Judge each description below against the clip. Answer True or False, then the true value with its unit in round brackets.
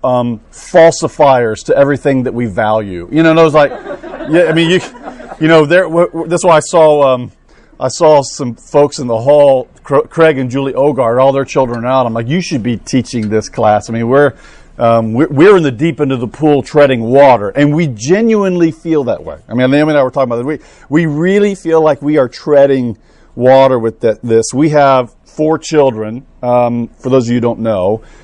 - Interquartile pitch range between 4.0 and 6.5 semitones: True (4.5 semitones)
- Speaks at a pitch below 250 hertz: True (140 Hz)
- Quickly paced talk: True (220 wpm)